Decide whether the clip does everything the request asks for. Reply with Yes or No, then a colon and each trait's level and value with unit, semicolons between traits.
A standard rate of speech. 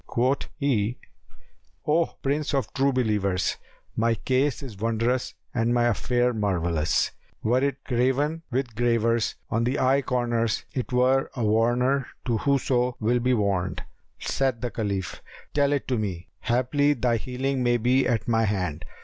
Yes: average, 150 wpm